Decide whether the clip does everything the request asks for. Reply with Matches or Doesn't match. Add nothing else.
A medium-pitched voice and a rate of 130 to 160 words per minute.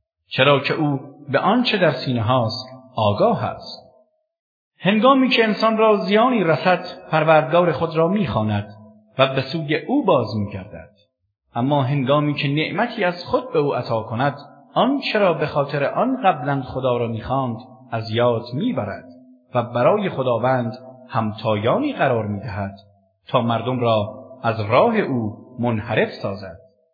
Doesn't match